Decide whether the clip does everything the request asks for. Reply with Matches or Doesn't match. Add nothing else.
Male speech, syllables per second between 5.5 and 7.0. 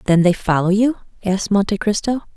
Doesn't match